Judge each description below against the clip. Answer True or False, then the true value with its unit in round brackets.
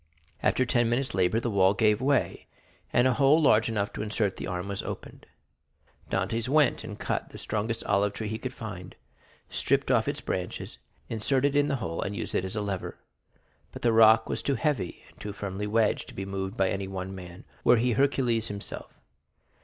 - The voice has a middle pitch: False (110 Hz)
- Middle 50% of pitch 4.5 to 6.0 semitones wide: False (3.7 semitones)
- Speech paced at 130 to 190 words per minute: False (200 wpm)